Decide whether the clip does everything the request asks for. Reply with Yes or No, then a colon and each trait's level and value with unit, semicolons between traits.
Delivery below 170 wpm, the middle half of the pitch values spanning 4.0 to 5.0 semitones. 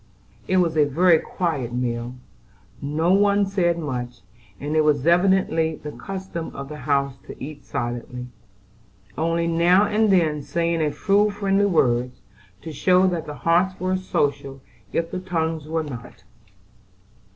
Yes: average, 150 wpm; average, 4.5 semitones